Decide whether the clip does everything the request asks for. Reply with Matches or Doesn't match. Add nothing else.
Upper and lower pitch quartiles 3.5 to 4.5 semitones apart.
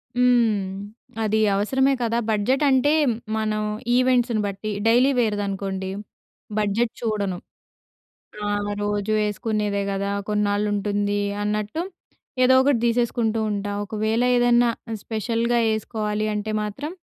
Doesn't match